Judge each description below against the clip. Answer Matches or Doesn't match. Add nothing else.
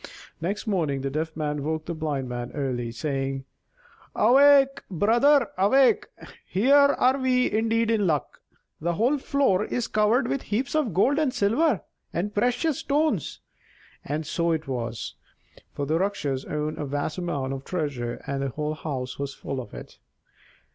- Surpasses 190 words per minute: Doesn't match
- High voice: Doesn't match